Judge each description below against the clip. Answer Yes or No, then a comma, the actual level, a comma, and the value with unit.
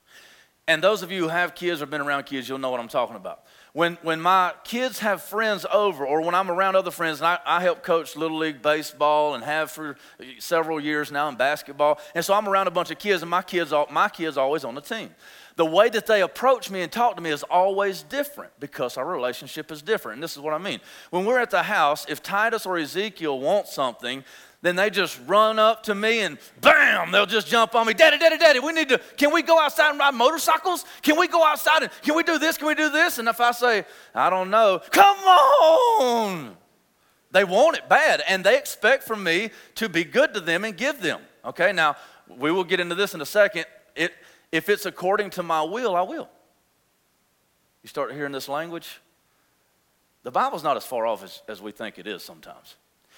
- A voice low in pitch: No, medium, 185 Hz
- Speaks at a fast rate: Yes, fast, 225 wpm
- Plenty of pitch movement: Yes, wide, 6.8 semitones